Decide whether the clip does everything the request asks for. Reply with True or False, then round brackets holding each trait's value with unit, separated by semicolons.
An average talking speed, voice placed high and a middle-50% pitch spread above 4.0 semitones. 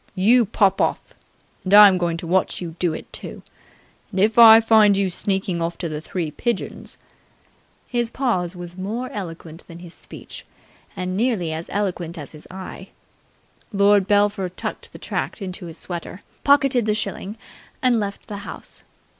False (170 wpm; 195 Hz; 3.4 semitones)